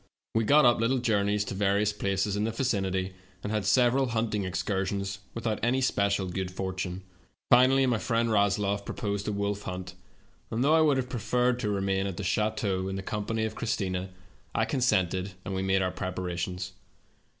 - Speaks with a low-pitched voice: Yes, low, 100 Hz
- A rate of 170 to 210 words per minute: Yes, average, 185 wpm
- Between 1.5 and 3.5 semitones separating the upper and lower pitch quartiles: Yes, average, 3.1 semitones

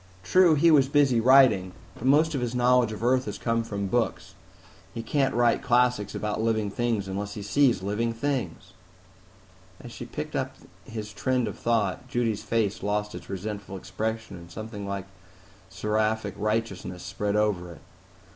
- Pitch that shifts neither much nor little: Yes, average, 3.3 semitones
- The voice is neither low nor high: No, low, 110 Hz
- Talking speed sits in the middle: Yes, average, 165 wpm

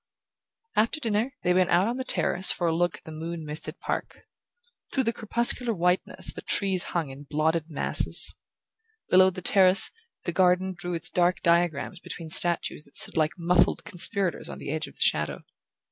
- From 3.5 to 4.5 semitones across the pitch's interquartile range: No, narrow, 2.6 semitones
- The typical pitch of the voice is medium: Yes, medium, 175 Hz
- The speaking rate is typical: Yes, average, 180 wpm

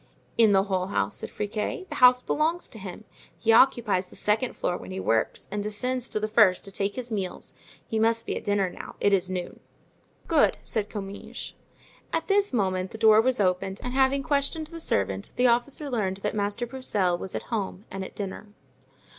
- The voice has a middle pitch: No, high, 215 Hz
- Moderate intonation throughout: Yes, average, 4.5 semitones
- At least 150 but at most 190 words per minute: No, average, 200 wpm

